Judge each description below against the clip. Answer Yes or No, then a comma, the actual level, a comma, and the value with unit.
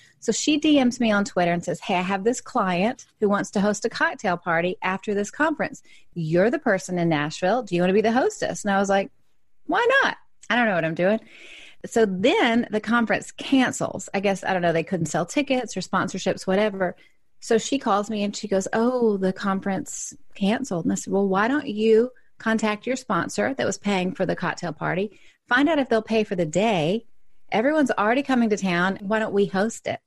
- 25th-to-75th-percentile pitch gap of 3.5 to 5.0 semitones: Yes, average, 4.0 semitones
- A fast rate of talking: Yes, fast, 220 wpm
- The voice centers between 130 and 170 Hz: No, high, 205 Hz